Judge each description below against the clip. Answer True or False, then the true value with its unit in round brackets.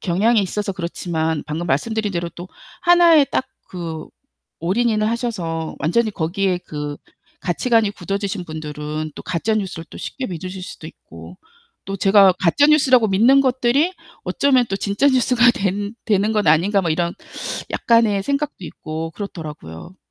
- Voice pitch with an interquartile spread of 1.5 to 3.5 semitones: False (5.5 semitones)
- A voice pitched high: True (195 Hz)